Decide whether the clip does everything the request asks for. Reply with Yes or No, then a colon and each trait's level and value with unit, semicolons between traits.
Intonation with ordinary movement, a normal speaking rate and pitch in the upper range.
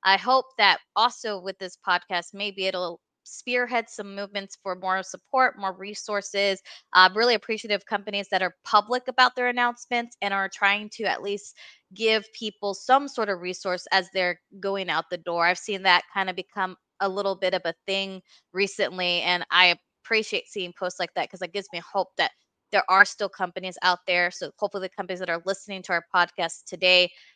No: narrow, 2.3 semitones; average, 195 wpm; high, 195 Hz